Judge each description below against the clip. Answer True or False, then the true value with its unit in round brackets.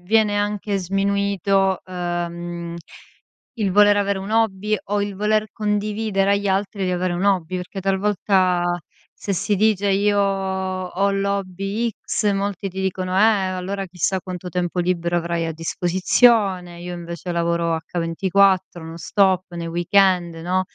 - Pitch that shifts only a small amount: True (2.2 semitones)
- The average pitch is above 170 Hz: True (190 Hz)